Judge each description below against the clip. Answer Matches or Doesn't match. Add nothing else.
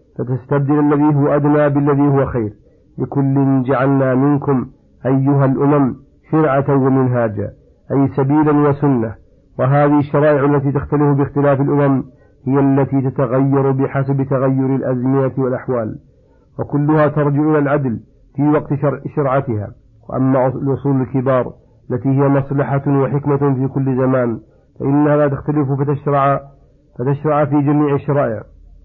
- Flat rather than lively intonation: Matches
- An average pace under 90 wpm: Doesn't match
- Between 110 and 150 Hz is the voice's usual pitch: Matches